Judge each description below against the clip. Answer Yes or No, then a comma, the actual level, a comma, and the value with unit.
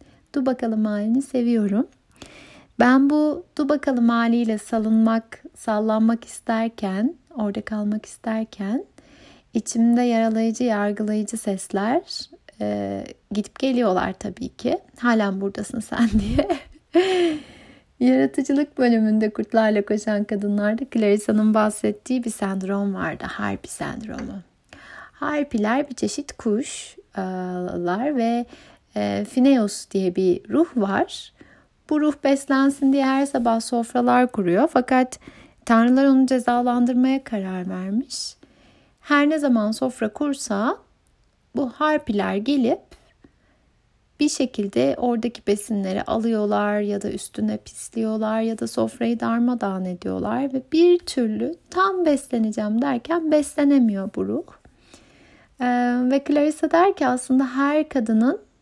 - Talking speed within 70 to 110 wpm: Yes, average, 105 wpm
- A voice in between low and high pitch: No, high, 235 Hz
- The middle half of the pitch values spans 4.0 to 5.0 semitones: Yes, average, 4.6 semitones